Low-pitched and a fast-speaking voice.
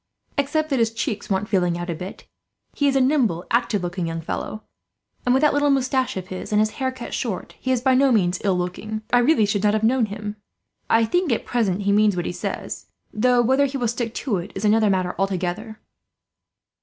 No: high, 220 Hz; fast, 225 wpm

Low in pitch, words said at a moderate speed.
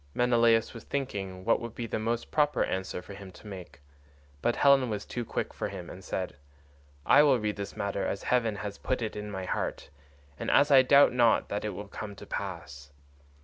No: low, 105 Hz; fast, 210 wpm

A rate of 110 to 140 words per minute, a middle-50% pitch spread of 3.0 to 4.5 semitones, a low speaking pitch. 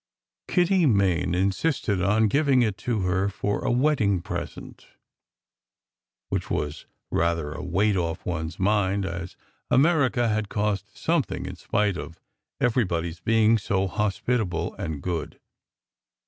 Yes: slow, 135 wpm; average, 4.2 semitones; low, 100 Hz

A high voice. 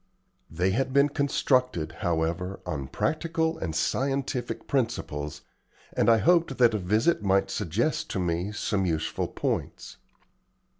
No: low, 105 Hz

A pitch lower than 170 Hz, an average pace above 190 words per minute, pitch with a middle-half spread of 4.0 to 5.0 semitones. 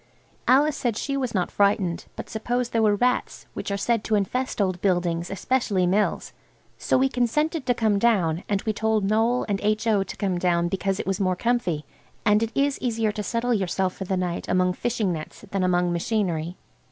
No: high, 205 Hz; average, 200 wpm; average, 4.3 semitones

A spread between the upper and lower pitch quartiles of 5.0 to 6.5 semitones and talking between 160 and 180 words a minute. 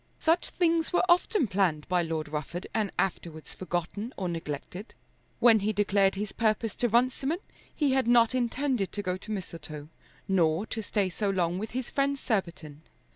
Yes: wide, 5.5 semitones; average, 170 wpm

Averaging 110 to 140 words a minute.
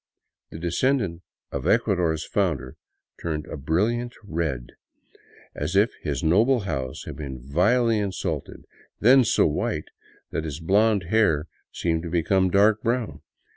Yes: slow, 135 wpm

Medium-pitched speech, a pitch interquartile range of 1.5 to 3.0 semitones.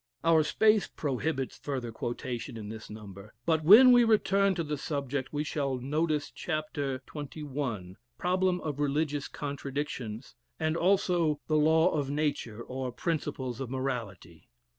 No: medium, 145 Hz; average, 3.8 semitones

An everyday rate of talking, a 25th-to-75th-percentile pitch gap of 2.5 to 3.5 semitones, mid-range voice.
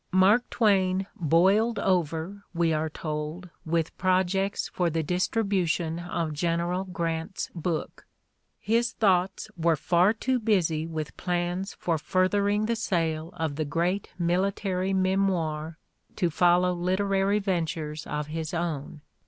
No: slow, 130 wpm; average, 3.0 semitones; medium, 175 Hz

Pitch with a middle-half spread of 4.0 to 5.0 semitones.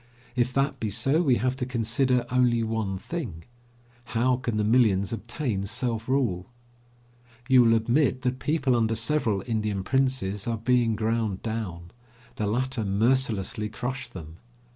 No: average, 3.1 semitones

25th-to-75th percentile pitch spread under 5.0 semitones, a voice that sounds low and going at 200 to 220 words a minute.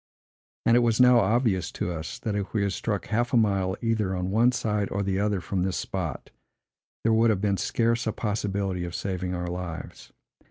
Yes: average, 3.4 semitones; low, 100 Hz; fast, 205 wpm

